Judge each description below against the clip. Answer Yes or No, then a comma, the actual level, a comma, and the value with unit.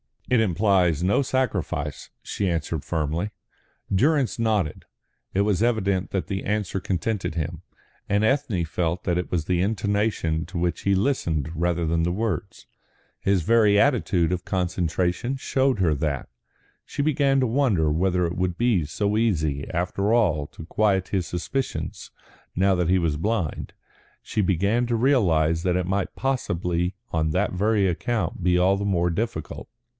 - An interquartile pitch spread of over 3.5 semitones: Yes, average, 4.3 semitones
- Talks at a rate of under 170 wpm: Yes, average, 160 wpm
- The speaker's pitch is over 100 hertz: No, very low, 95 Hz